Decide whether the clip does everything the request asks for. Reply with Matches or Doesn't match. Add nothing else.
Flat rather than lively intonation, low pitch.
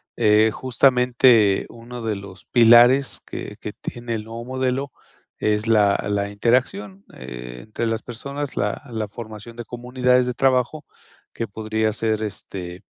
Doesn't match